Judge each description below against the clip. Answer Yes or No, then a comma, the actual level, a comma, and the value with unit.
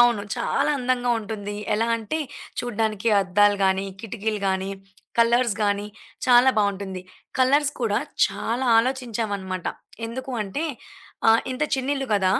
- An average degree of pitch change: Yes, average, 3.6 semitones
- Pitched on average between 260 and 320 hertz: No, high, 225 Hz